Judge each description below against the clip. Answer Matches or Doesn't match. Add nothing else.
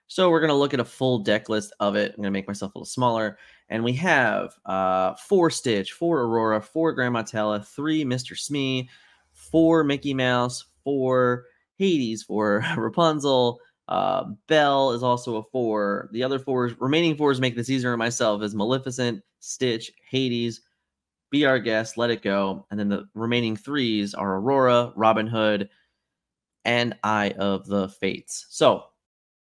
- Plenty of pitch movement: Doesn't match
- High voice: Doesn't match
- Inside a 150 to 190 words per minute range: Matches